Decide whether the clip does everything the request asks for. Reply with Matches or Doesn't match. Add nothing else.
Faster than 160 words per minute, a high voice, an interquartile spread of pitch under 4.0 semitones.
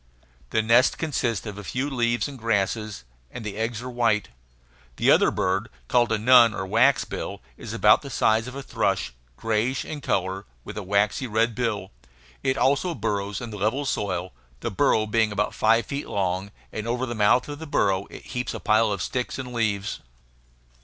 Doesn't match